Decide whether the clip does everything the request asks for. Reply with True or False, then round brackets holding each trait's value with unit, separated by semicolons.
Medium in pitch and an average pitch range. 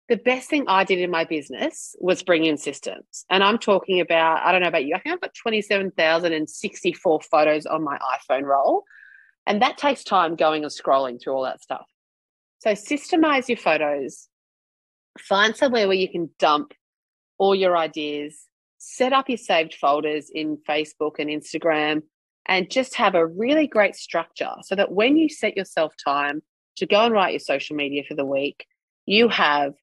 False (175 Hz; 6.1 semitones)